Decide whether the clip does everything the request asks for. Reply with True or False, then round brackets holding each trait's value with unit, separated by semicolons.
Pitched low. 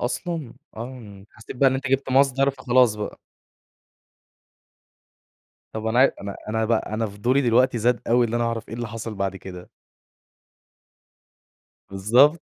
True (120 Hz)